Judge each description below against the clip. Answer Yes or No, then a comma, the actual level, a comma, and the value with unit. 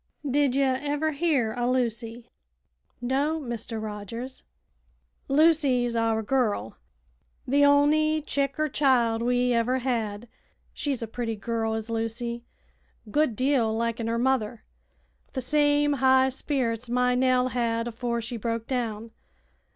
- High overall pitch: Yes, high, 245 Hz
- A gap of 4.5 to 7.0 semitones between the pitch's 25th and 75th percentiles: No, average, 3.1 semitones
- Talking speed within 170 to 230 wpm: No, slow, 135 wpm